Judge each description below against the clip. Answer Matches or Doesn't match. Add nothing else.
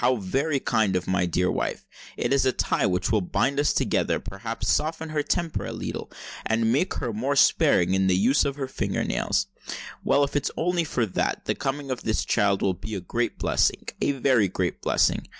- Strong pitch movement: Matches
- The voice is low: Matches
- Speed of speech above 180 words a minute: Matches